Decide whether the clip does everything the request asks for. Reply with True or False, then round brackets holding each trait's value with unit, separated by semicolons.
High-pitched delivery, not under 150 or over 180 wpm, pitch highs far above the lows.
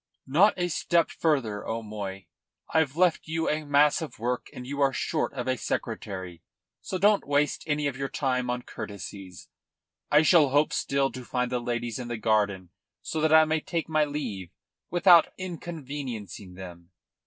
False (135 Hz; 170 wpm; 6.0 semitones)